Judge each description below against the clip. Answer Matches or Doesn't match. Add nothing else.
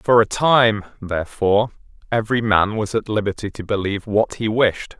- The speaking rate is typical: Matches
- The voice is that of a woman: Doesn't match